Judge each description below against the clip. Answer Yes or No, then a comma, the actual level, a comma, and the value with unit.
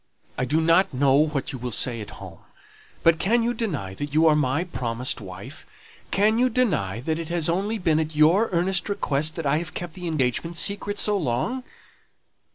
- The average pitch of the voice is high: No, medium, 160 Hz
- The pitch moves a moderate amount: No, wide, 6.4 semitones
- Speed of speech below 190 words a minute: No, average, 195 wpm